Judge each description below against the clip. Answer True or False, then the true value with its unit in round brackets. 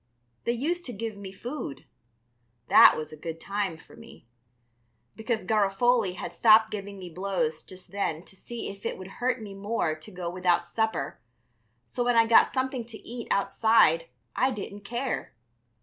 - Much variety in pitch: False (4.3 semitones)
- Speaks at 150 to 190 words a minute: True (170 wpm)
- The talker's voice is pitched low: False (200 Hz)